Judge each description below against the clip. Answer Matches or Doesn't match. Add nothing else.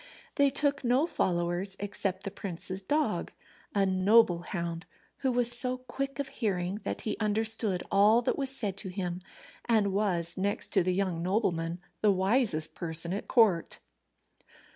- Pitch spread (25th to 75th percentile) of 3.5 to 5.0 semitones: Matches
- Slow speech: Doesn't match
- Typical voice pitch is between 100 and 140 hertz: Doesn't match